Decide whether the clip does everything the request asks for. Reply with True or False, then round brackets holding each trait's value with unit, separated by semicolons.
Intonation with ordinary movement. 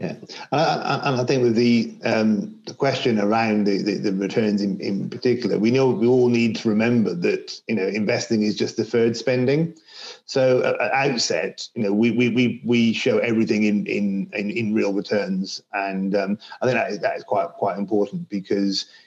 True (3.5 semitones)